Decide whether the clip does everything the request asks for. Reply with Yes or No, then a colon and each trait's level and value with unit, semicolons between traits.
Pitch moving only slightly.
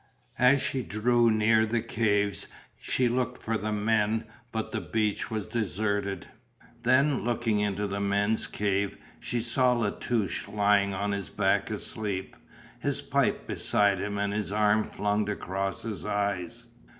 Yes: narrow, 2.0 semitones